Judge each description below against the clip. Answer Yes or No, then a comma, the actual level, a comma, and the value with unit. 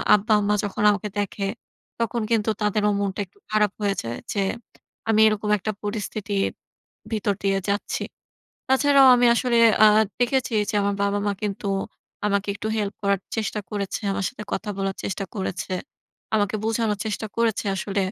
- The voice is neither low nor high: No, high, 210 Hz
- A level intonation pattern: Yes, narrow, 1.6 semitones